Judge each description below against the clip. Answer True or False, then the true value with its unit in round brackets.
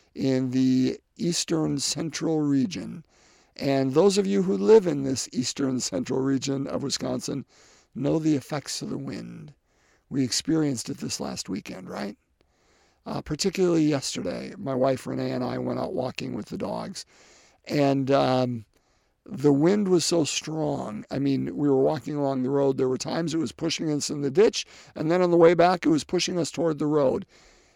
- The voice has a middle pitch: True (145 Hz)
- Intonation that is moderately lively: True (3.6 semitones)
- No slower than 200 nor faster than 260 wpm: False (180 wpm)